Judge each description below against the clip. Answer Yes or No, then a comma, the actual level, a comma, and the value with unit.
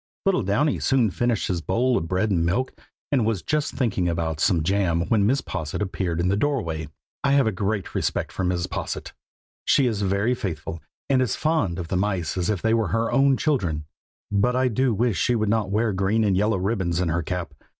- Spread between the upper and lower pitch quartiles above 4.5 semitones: Yes, average, 5.3 semitones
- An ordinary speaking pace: No, fast, 215 wpm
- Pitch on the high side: No, low, 100 Hz